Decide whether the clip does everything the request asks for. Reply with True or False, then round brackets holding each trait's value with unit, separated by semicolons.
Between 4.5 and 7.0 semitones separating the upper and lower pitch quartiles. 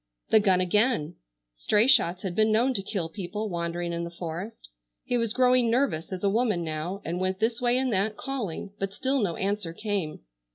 True (4.8 semitones)